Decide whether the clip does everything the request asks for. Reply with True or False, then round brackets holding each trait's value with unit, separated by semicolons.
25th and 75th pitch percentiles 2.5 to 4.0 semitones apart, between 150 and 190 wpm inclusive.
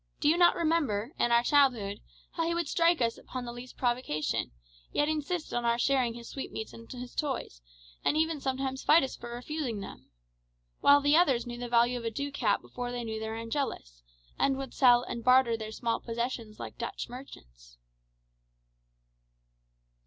True (3.5 semitones; 175 wpm)